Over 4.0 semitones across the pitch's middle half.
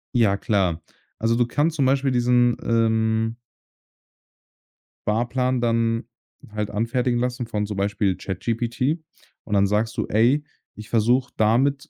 No: average, 2.7 semitones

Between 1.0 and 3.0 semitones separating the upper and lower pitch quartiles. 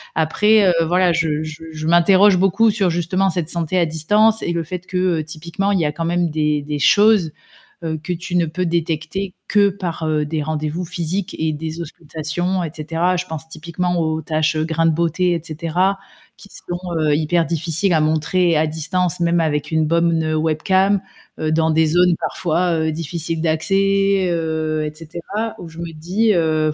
Yes: narrow, 2.5 semitones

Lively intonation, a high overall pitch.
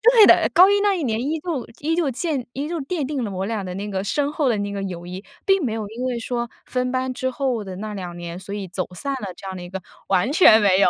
Yes: wide, 6.4 semitones; high, 230 Hz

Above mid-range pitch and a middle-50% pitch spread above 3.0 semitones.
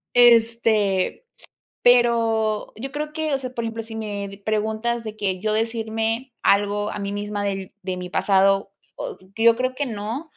No: high, 220 Hz; narrow, 2.6 semitones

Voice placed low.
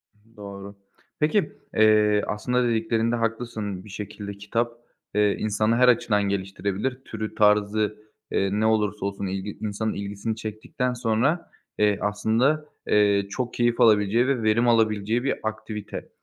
Yes: low, 110 Hz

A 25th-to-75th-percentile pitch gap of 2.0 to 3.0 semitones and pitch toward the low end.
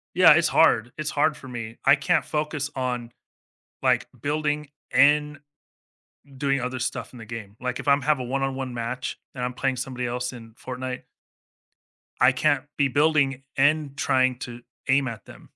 Yes: narrow, 2.6 semitones; low, 130 Hz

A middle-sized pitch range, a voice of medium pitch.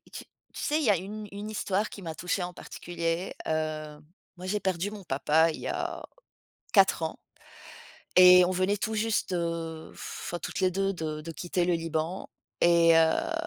Yes: average, 3.1 semitones; medium, 175 Hz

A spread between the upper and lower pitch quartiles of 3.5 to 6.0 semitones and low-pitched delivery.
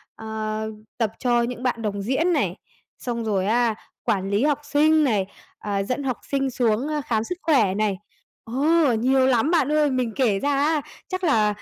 No: average, 4.8 semitones; high, 245 Hz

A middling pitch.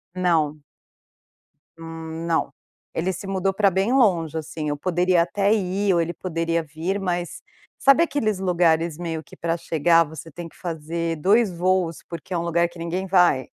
Yes: medium, 170 Hz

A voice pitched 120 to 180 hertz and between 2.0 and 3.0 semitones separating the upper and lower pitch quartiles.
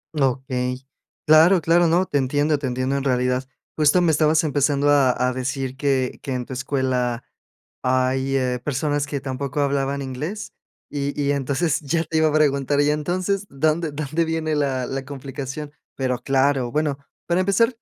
Yes: medium, 140 Hz; average, 2.7 semitones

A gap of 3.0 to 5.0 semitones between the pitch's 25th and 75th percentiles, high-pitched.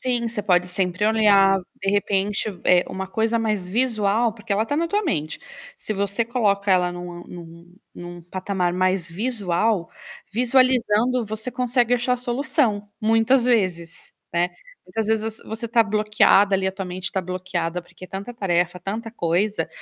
Yes: average, 4.0 semitones; high, 205 Hz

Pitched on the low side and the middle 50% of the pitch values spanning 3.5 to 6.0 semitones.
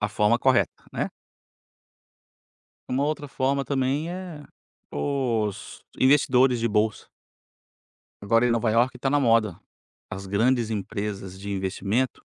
Yes: low, 120 Hz; average, 4.2 semitones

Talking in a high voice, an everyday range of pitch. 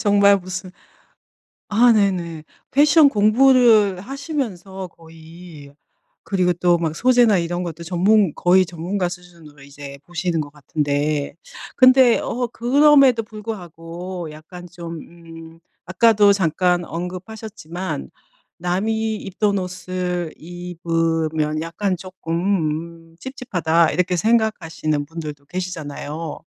No: medium, 180 Hz; average, 3.9 semitones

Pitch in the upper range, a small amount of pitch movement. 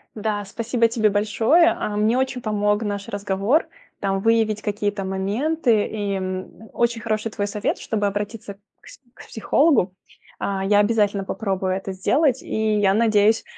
Yes: high, 210 Hz; narrow, 2.1 semitones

